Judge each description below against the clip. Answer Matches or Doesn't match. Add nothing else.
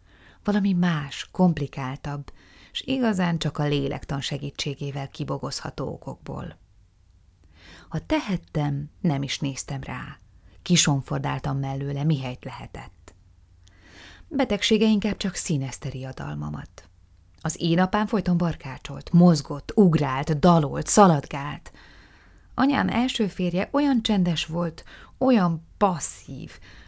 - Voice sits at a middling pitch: Matches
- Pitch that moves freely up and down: Matches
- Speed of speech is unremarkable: Doesn't match